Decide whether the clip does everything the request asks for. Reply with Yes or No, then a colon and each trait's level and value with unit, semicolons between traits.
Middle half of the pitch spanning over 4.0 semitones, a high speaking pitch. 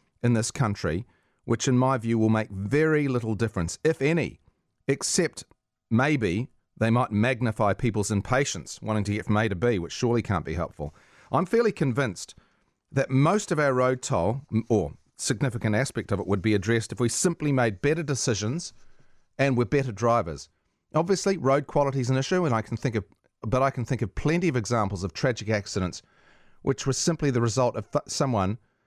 No: average, 4.4 semitones; low, 120 Hz